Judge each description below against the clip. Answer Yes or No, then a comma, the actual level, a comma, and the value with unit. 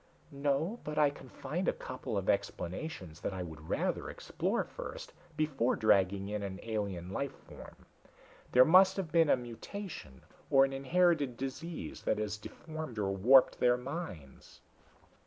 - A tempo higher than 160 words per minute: No, average, 155 wpm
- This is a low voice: Yes, low, 125 Hz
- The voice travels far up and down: Yes, wide, 7.6 semitones